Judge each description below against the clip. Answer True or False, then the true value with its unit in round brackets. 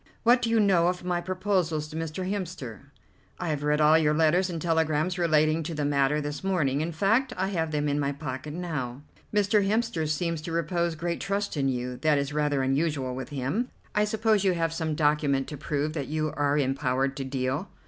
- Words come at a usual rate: False (210 wpm)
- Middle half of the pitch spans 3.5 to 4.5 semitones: True (3.8 semitones)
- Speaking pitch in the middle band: True (155 Hz)